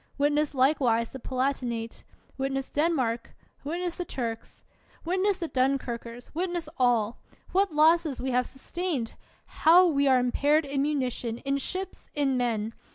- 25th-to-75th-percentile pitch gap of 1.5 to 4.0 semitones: No, average, 4.6 semitones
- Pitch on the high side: Yes, very high, 275 Hz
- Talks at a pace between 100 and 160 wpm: Yes, average, 145 wpm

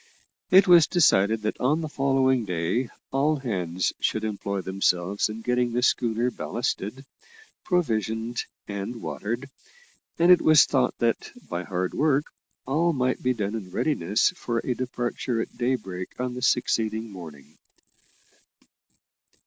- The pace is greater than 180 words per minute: No, slow, 135 wpm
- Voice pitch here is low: Yes, low, 120 Hz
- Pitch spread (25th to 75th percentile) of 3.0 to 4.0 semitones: No, average, 4.6 semitones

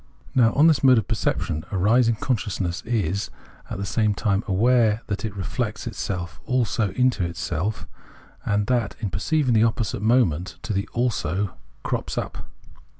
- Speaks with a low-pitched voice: Yes, low, 105 Hz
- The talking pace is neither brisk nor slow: Yes, average, 165 wpm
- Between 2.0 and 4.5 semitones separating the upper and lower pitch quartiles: Yes, average, 3.6 semitones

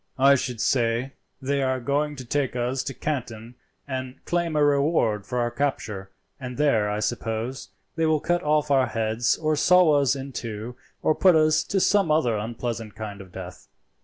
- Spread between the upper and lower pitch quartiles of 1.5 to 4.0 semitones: No, average, 4.5 semitones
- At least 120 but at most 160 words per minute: No, average, 185 wpm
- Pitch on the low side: Yes, low, 130 Hz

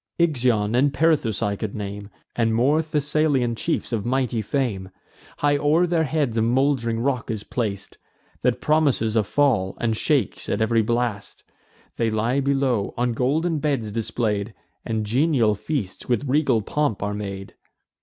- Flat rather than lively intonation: No, average, 4.8 semitones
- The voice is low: Yes, low, 120 Hz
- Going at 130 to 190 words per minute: Yes, average, 155 wpm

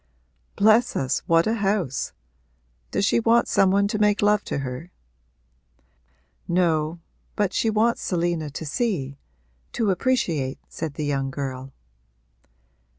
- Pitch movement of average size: No, wide, 6.5 semitones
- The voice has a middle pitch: Yes, medium, 175 Hz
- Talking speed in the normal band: No, slow, 130 wpm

